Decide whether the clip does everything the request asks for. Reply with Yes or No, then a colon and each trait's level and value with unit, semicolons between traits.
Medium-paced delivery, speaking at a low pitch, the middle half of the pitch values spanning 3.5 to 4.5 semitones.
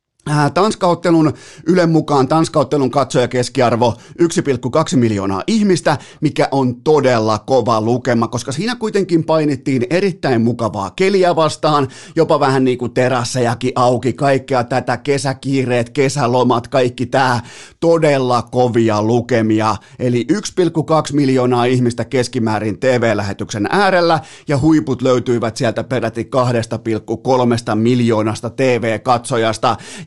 Yes: average, 105 wpm; low, 130 Hz; average, 4.0 semitones